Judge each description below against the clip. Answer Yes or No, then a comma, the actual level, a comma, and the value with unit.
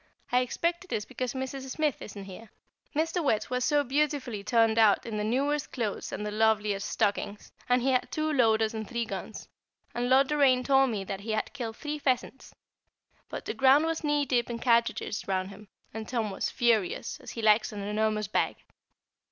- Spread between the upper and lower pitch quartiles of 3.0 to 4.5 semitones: Yes, average, 4.0 semitones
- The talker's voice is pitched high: Yes, high, 235 Hz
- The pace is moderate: Yes, average, 195 wpm